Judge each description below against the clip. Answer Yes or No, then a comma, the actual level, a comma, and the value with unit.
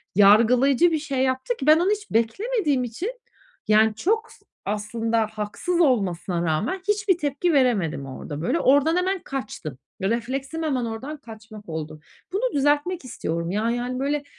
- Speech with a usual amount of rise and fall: No, wide, 7.1 semitones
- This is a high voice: Yes, very high, 255 Hz